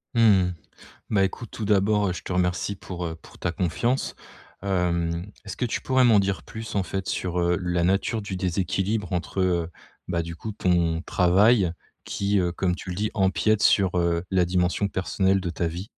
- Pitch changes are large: No, narrow, 2.5 semitones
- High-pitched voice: No, very low, 95 Hz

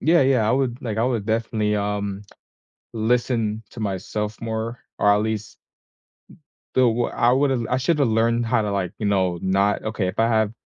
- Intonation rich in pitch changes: No, narrow, 2.6 semitones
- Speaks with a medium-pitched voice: No, low, 110 Hz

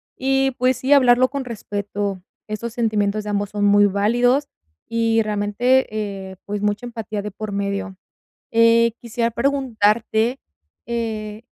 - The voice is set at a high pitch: Yes, high, 220 Hz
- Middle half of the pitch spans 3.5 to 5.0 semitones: No, average, 2.9 semitones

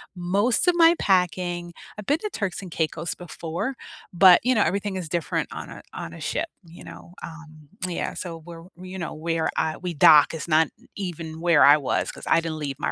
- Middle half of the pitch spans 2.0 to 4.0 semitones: Yes, average, 2.8 semitones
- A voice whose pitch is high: No, medium, 175 Hz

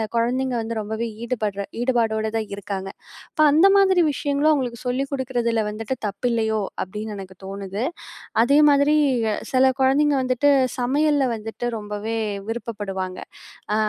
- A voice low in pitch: No, high, 230 Hz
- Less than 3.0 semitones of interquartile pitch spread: No, average, 3.9 semitones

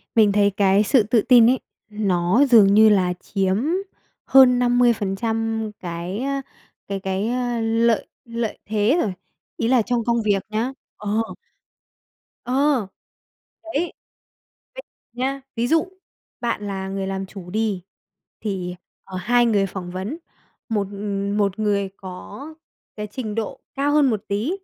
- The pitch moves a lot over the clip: No, average, 3.5 semitones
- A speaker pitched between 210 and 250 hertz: Yes, high, 215 Hz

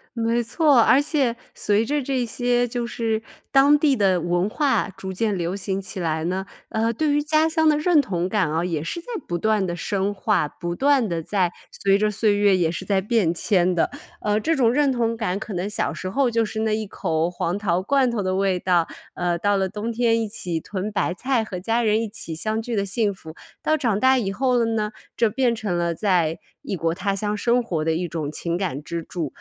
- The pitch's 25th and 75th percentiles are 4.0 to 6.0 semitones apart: Yes, average, 4.7 semitones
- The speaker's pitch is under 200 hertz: No, high, 205 Hz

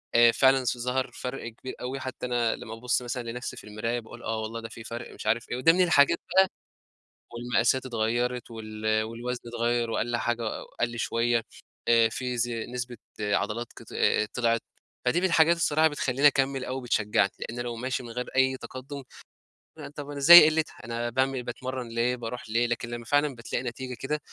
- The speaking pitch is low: Yes, low, 120 Hz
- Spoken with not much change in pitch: Yes, narrow, 2.1 semitones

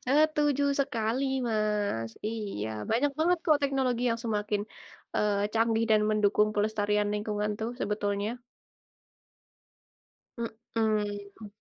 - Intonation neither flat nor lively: No, narrow, 2.2 semitones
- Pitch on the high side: Yes, high, 215 Hz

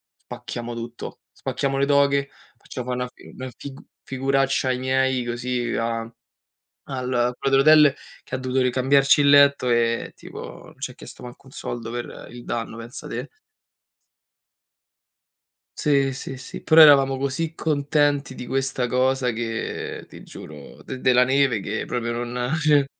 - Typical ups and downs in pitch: No, narrow, 2.3 semitones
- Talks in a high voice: No, low, 130 Hz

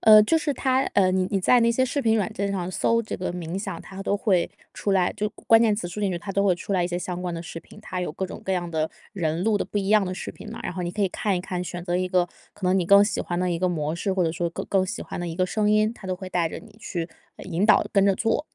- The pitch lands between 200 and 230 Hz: No, high, 190 Hz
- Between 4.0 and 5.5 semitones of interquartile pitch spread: No, average, 2.9 semitones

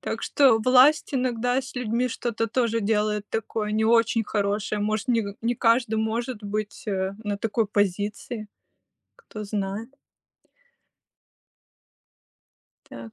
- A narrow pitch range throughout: Yes, narrow, 2.3 semitones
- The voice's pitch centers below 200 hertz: No, high, 220 Hz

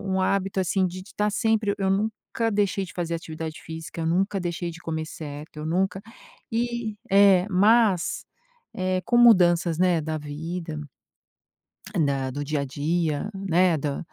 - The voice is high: No, medium, 180 Hz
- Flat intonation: No, average, 3.7 semitones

